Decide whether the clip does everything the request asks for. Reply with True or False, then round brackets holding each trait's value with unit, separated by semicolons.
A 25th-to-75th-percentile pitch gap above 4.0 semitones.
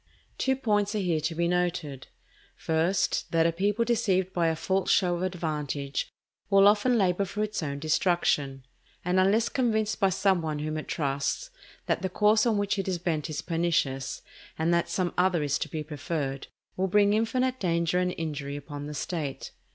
True (4.5 semitones)